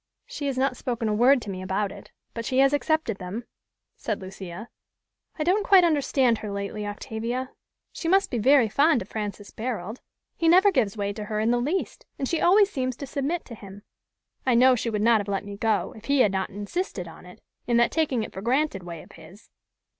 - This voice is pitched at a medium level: No, high, 235 Hz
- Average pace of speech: No, fast, 220 wpm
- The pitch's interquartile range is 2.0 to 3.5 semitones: No, wide, 5.4 semitones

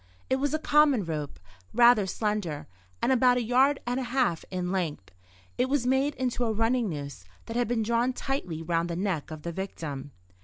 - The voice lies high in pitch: Yes, high, 225 Hz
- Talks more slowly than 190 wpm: No, average, 195 wpm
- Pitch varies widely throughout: Yes, wide, 7.1 semitones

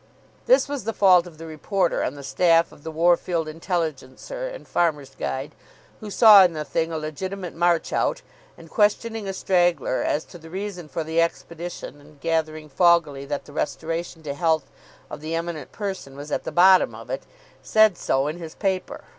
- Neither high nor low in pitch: Yes, medium, 165 Hz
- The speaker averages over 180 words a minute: Yes, average, 190 wpm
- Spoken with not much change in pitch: No, average, 3.3 semitones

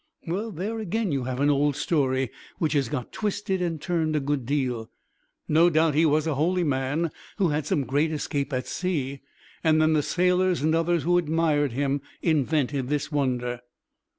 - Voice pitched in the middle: Yes, medium, 150 Hz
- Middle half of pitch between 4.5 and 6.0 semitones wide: No, average, 3.5 semitones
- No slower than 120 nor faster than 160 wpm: No, average, 180 wpm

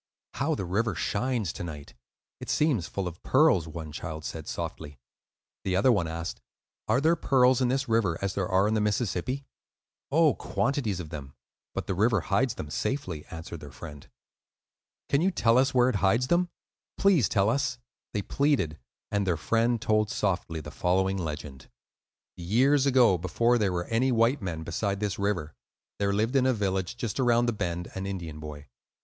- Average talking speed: Yes, average, 180 wpm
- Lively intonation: Yes, wide, 6.3 semitones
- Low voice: Yes, low, 100 Hz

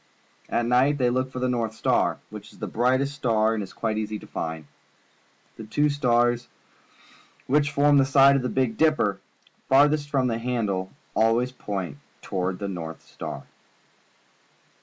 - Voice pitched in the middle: No, low, 120 Hz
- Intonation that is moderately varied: Yes, average, 3.9 semitones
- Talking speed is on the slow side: No, average, 175 wpm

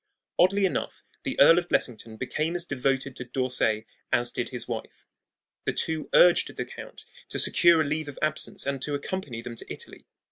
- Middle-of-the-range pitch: Yes, medium, 145 Hz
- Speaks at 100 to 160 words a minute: No, average, 185 wpm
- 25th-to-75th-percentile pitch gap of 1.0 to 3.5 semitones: No, wide, 5.5 semitones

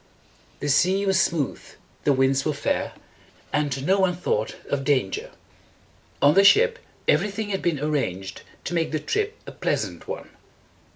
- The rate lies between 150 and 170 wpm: Yes, average, 165 wpm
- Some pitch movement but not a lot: No, wide, 5.9 semitones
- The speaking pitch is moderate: Yes, medium, 155 Hz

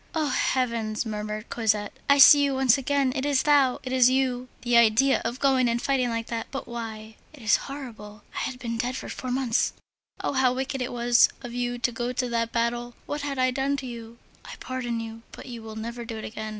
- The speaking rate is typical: No, fast, 230 wpm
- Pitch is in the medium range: No, high, 245 Hz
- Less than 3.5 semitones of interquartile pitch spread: Yes, narrow, 2.4 semitones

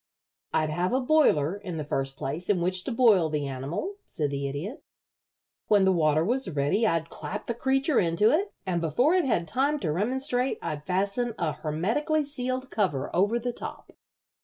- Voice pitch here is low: No, high, 190 Hz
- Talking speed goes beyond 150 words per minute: Yes, average, 185 wpm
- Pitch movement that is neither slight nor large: No, wide, 8.1 semitones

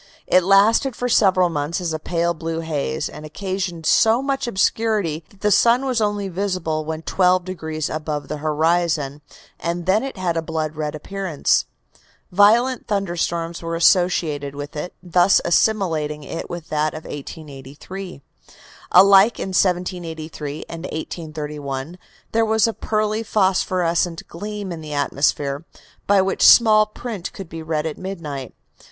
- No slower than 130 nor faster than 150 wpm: Yes, average, 145 wpm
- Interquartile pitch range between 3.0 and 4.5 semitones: Yes, average, 4.1 semitones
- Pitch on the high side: No, medium, 170 Hz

